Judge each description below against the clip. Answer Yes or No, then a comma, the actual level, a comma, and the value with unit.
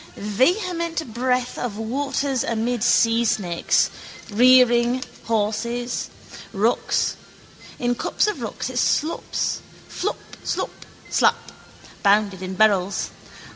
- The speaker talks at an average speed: No, slow, 95 wpm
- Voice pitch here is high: Yes, high, 235 Hz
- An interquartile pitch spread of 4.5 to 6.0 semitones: No, average, 3.1 semitones